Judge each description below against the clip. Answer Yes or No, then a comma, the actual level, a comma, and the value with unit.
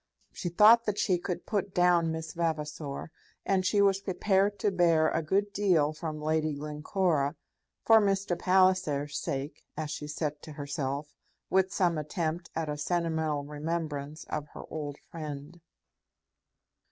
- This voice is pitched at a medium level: Yes, medium, 160 Hz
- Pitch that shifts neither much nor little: Yes, average, 3.8 semitones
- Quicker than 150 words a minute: No, average, 145 wpm